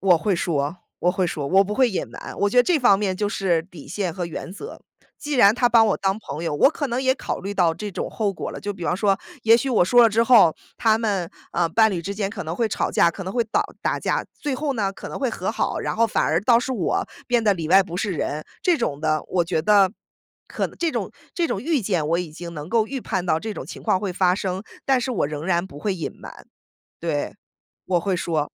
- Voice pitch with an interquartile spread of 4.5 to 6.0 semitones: Yes, average, 4.8 semitones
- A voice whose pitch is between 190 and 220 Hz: Yes, high, 195 Hz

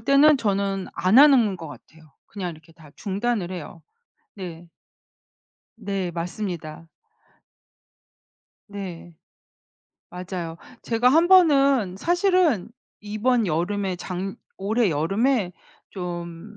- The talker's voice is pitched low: No, high, 195 Hz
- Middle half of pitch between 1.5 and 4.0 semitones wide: No, wide, 5.4 semitones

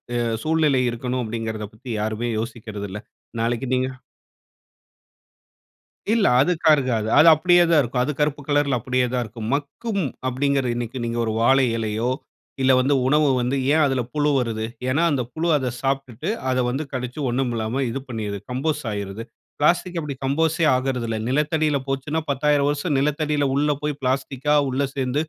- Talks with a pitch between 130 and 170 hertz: Yes, low, 135 Hz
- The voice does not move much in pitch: No, average, 3.6 semitones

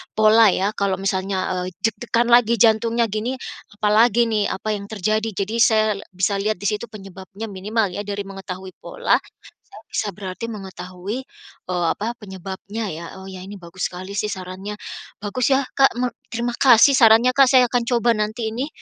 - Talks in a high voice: Yes, high, 210 Hz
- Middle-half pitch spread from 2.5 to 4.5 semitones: Yes, average, 3.1 semitones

